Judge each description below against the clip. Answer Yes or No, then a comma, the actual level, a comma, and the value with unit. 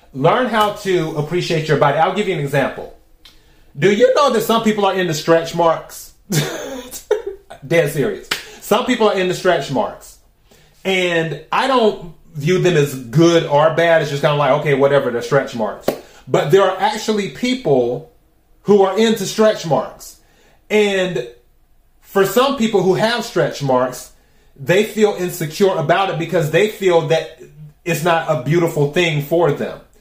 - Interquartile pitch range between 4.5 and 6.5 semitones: Yes, average, 4.8 semitones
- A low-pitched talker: No, medium, 175 Hz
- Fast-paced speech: No, average, 165 wpm